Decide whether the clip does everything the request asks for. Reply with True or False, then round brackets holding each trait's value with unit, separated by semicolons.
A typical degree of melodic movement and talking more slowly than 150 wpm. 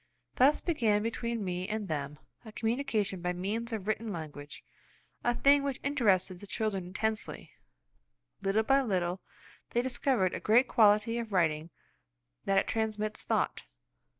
True (4.1 semitones; 140 wpm)